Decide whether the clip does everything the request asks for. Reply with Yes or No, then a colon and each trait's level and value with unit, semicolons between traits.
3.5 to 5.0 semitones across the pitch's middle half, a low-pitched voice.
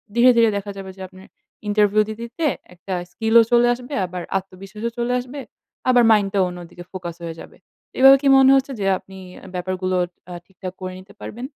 No: average, 4.3 semitones; high, 200 Hz